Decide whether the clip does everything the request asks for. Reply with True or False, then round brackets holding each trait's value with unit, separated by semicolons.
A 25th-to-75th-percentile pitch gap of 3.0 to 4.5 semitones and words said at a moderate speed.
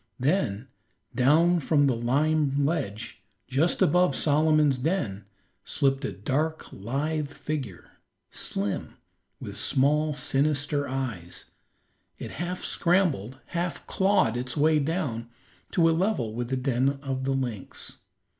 False (3.9 semitones; 120 wpm)